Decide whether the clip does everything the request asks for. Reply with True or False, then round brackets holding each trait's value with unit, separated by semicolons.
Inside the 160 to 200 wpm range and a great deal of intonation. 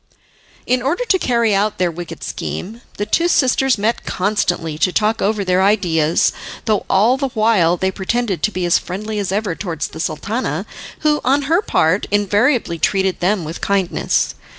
False (175 wpm; 4.5 semitones)